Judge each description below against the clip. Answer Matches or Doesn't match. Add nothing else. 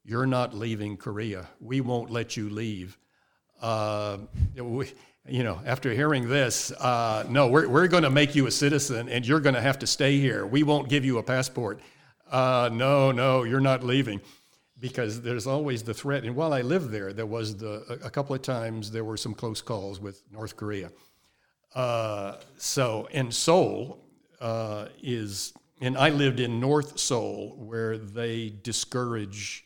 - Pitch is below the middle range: Matches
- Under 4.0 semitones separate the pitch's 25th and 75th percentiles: Matches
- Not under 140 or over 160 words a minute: Doesn't match